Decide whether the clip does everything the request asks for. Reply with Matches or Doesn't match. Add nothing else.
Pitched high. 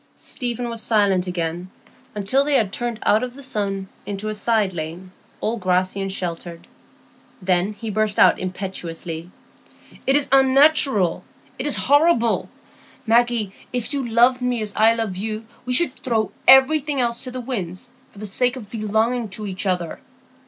Matches